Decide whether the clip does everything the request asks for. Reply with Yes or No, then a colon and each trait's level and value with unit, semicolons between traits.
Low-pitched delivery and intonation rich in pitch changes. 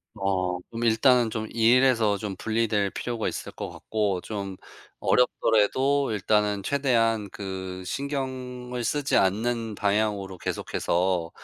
No: low, 110 Hz; average, 3.9 semitones